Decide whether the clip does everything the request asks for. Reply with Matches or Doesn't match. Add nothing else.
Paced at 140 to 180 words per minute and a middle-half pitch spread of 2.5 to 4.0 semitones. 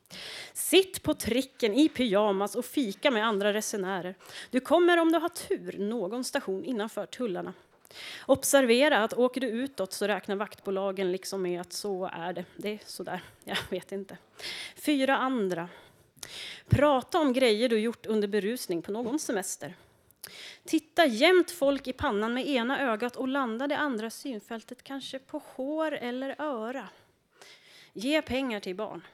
Doesn't match